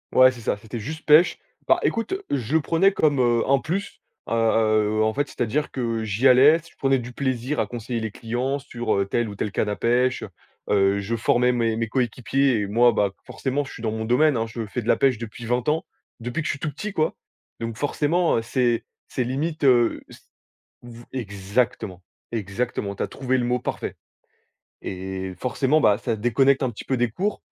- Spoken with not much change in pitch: No, average, 3.6 semitones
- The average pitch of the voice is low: Yes, low, 120 Hz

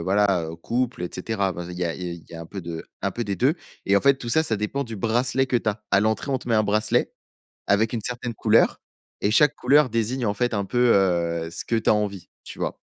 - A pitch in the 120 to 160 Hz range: No, low, 110 Hz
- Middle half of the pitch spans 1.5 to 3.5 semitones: No, average, 4.2 semitones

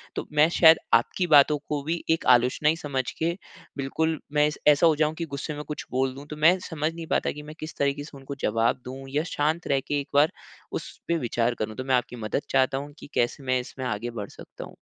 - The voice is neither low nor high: Yes, medium, 145 Hz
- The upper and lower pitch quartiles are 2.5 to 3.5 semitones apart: Yes, average, 3.1 semitones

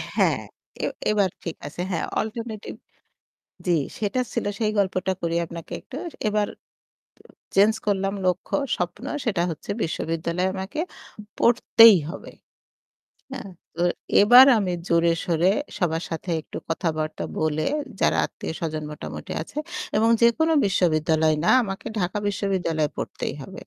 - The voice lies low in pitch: No, medium, 185 Hz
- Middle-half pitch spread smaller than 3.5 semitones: No, average, 4.1 semitones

